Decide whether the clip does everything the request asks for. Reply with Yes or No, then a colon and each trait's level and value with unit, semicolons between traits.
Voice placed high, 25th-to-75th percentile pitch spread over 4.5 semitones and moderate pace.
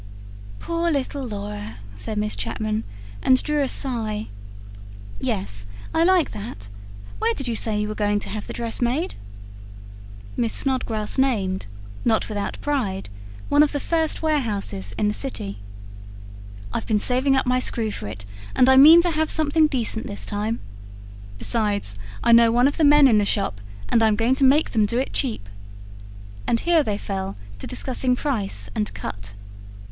Yes: high, 230 Hz; average, 5.0 semitones; average, 170 wpm